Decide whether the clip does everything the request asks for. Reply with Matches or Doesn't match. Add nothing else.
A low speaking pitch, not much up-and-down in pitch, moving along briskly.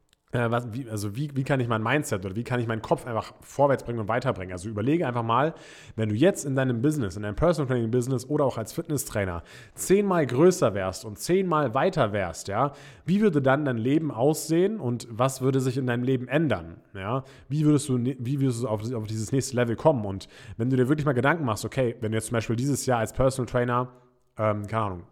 Doesn't match